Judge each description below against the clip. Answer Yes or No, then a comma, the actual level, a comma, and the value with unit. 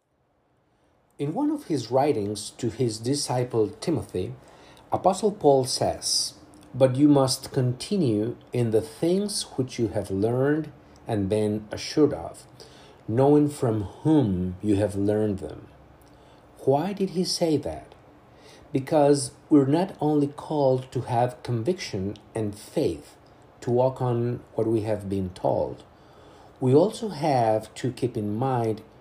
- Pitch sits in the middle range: No, low, 130 Hz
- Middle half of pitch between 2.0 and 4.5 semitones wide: No, average, 5.2 semitones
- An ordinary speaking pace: No, slow, 130 wpm